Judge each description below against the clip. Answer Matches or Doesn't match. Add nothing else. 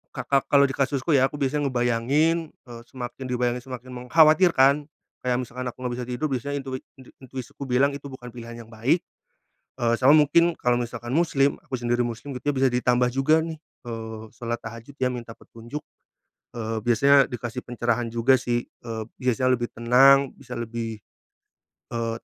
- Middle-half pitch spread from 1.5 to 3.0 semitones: Matches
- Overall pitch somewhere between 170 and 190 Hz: Doesn't match